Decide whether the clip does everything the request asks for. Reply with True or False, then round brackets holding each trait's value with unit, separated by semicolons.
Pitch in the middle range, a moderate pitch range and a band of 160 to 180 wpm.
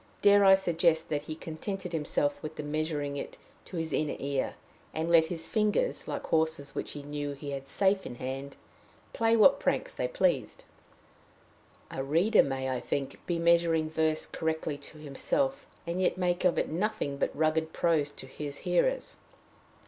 True (160 Hz; 3.8 semitones; 170 wpm)